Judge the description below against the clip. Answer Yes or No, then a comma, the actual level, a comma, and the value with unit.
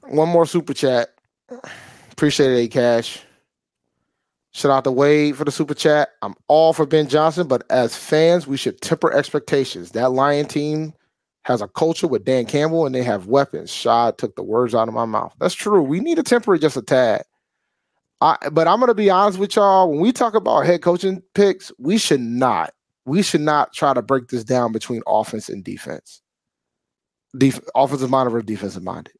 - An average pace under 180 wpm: No, average, 190 wpm